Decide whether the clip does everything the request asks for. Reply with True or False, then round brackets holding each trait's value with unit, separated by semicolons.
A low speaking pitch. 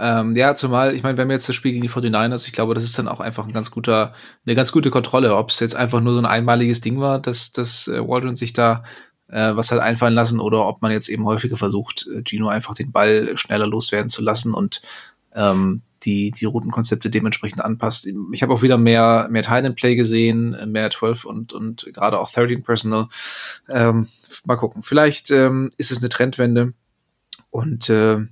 True (115 Hz)